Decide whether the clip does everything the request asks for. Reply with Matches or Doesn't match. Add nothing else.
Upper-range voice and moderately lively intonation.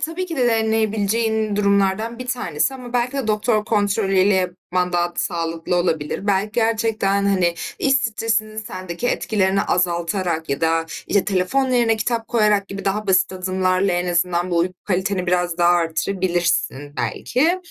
Matches